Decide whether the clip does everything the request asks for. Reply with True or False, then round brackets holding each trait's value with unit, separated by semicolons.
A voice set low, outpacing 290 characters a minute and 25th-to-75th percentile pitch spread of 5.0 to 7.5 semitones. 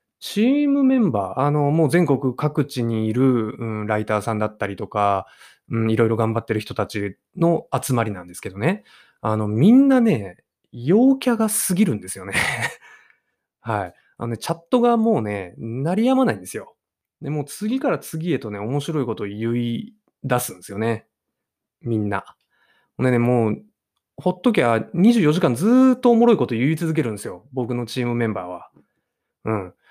False (125 Hz; 335 characters per minute; 8.8 semitones)